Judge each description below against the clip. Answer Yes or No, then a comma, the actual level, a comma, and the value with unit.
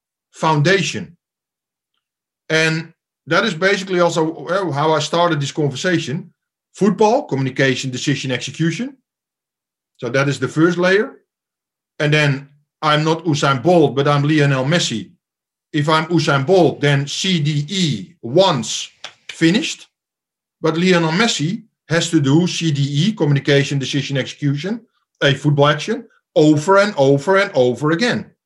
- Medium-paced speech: No, slow, 120 wpm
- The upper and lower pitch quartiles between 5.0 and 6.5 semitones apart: No, average, 3.9 semitones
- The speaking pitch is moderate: Yes, medium, 160 Hz